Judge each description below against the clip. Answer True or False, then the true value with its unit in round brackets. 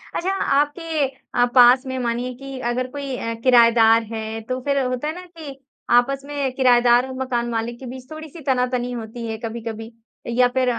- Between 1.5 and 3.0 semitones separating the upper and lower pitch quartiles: True (2.4 semitones)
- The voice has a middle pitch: False (250 Hz)